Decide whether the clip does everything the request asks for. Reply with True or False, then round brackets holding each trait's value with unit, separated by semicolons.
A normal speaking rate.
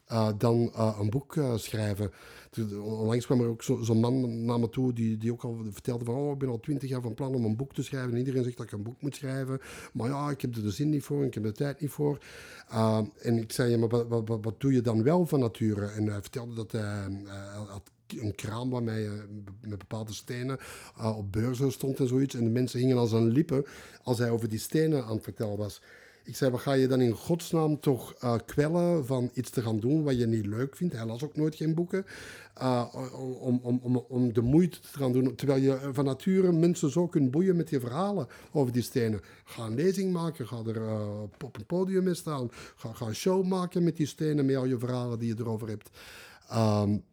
False (245 wpm)